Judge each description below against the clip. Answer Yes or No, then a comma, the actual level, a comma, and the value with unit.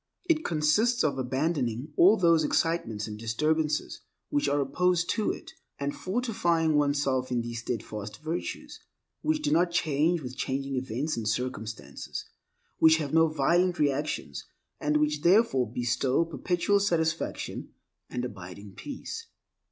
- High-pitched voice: No, medium, 150 Hz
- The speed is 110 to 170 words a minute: Yes, slow, 135 wpm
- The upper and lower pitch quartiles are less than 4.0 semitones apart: No, average, 5.3 semitones